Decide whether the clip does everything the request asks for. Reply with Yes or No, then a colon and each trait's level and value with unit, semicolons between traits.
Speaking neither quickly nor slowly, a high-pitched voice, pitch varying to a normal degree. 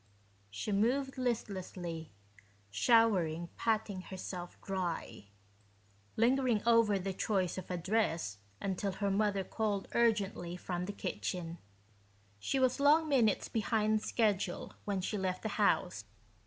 No: slow, 120 wpm; high, 200 Hz; average, 3.7 semitones